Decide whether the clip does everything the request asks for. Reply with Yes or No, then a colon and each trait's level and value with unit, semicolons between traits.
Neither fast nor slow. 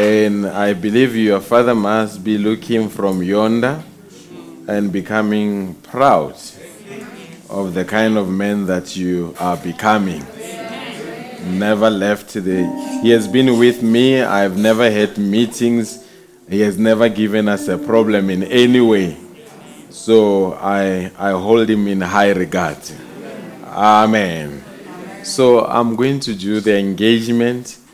No: slow, 130 wpm